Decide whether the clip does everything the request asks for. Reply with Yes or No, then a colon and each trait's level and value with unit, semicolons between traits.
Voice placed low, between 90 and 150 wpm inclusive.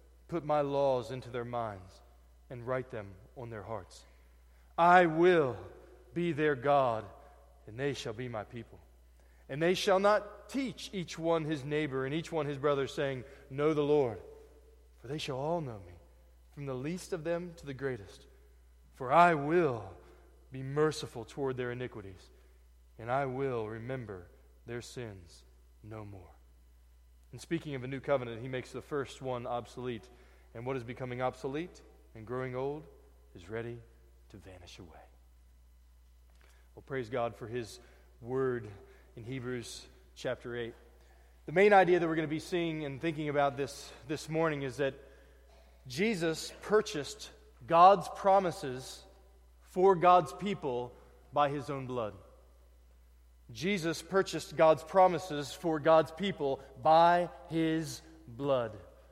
Yes: low, 130 Hz; average, 145 wpm